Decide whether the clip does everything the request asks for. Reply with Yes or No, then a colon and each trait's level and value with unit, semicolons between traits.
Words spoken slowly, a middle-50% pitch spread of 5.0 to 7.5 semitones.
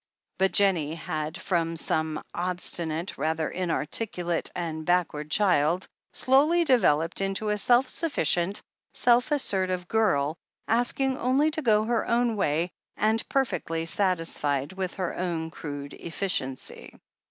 Yes: slow, 120 wpm; wide, 5.6 semitones